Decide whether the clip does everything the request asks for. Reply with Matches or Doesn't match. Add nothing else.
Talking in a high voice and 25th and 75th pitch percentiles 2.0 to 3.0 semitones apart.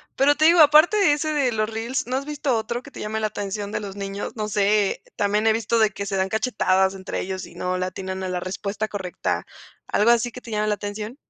Doesn't match